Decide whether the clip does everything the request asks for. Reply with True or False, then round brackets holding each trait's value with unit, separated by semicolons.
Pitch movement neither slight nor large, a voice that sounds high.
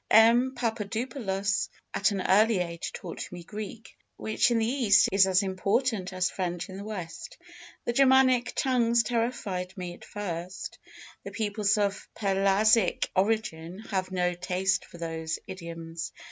True (3.6 semitones; 200 Hz)